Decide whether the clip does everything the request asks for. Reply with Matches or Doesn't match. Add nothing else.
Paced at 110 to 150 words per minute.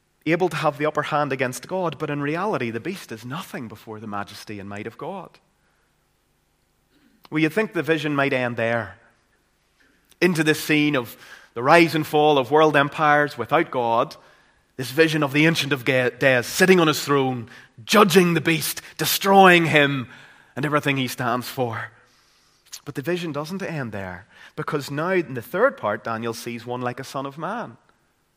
Doesn't match